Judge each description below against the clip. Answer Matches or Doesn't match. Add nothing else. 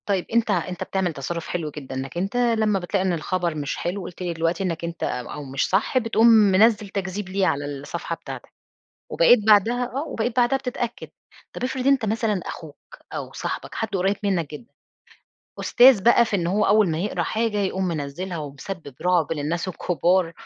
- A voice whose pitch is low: Doesn't match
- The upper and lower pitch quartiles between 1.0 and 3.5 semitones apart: Doesn't match